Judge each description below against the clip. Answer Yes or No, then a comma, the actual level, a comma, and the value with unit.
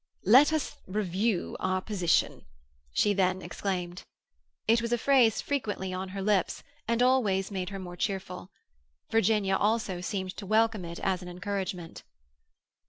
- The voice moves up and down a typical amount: Yes, average, 3.2 semitones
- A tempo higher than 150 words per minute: No, average, 145 wpm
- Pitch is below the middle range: No, high, 195 Hz